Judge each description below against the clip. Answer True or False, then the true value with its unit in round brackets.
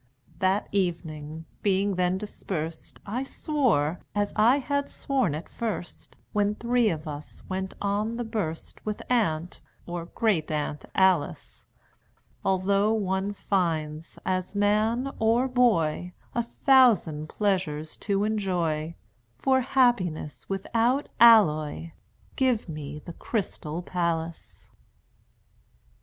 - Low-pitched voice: False (190 Hz)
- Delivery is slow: True (110 wpm)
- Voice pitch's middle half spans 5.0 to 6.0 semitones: True (5.5 semitones)